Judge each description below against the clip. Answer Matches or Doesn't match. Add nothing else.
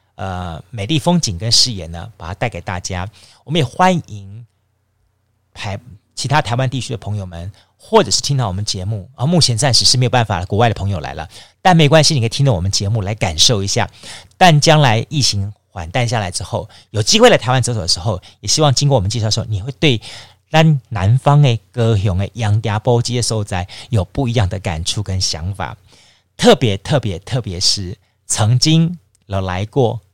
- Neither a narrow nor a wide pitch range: Matches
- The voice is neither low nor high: Doesn't match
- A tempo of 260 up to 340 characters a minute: Matches